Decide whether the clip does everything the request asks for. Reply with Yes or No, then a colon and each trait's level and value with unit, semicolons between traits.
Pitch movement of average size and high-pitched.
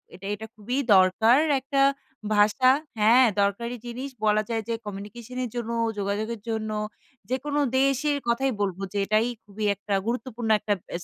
Yes: average, 3.5 semitones; high, 225 Hz